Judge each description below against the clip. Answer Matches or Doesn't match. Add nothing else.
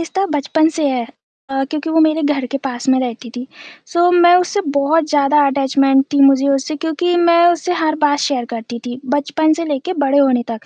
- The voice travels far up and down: Doesn't match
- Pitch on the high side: Matches